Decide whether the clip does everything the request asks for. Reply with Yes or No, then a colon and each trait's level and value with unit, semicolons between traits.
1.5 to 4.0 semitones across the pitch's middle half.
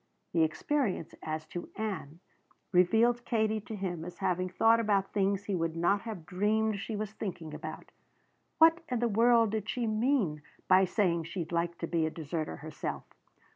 No: average, 4.5 semitones